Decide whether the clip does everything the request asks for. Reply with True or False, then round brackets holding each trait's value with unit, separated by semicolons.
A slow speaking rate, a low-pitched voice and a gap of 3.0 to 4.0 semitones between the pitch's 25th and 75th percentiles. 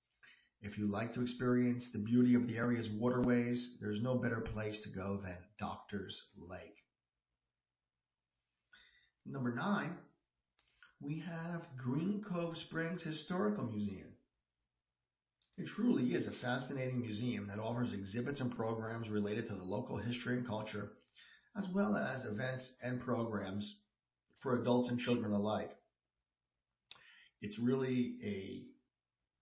True (125 wpm; 115 Hz; 3.4 semitones)